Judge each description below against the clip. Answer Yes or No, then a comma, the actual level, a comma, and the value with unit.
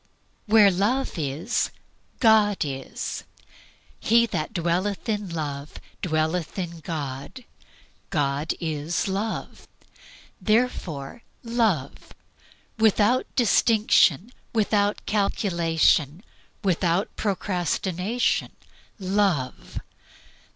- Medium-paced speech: No, slow, 75 wpm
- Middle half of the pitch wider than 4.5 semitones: Yes, average, 5.1 semitones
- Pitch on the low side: No, medium, 185 Hz